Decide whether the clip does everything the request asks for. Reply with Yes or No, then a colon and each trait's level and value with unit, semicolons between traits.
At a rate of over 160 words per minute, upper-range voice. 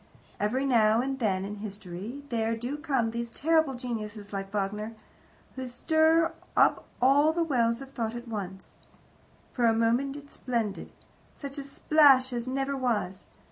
No: average, 155 wpm; high, 240 Hz